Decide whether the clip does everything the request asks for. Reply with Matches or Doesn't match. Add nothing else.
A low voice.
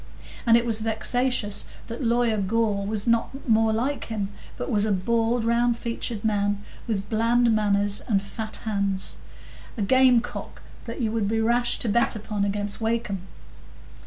Doesn't match